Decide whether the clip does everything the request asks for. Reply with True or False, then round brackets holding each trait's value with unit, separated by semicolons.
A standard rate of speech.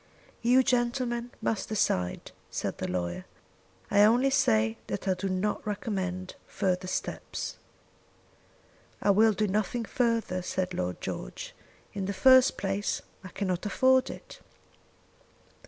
False (125 wpm)